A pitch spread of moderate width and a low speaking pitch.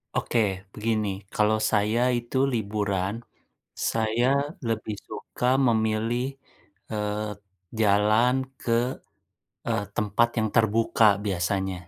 No: narrow, 1.7 semitones; low, 110 Hz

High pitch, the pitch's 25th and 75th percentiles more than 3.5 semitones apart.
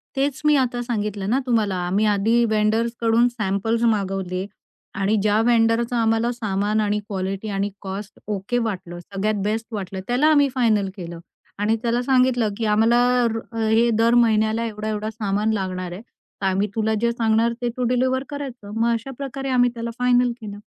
No: high, 220 Hz; average, 2.7 semitones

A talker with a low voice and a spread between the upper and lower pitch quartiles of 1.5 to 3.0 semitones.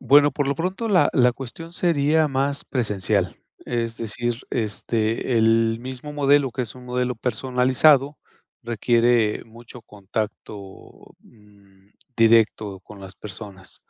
No: low, 120 Hz; average, 4.0 semitones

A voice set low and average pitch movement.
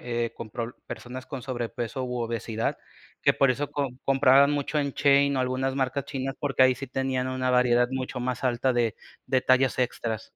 No: low, 130 Hz; narrow, 1.7 semitones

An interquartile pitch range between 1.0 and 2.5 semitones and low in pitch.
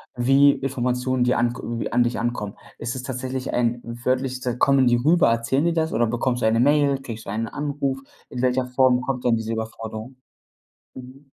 Yes: narrow, 2.2 semitones; low, 125 Hz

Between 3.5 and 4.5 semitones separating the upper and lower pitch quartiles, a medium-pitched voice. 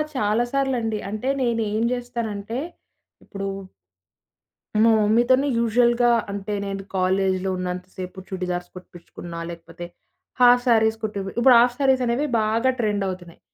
No: average, 4.2 semitones; high, 215 Hz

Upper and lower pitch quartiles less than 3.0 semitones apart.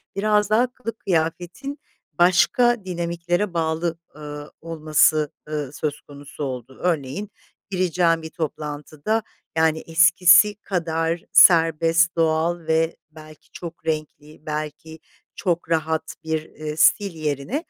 Yes: narrow, 2.4 semitones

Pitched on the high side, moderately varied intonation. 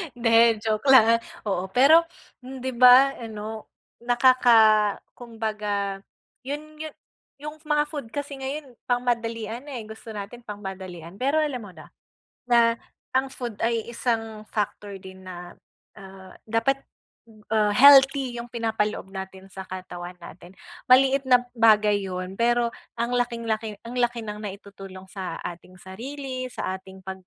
Yes: high, 230 Hz; average, 4.1 semitones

